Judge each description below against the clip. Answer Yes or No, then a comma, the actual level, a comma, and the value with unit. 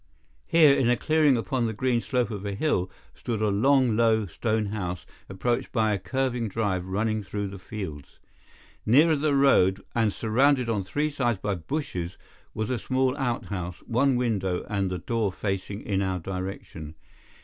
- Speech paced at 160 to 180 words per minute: Yes, average, 170 wpm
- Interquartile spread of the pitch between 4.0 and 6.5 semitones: Yes, average, 4.7 semitones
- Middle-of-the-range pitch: No, low, 110 Hz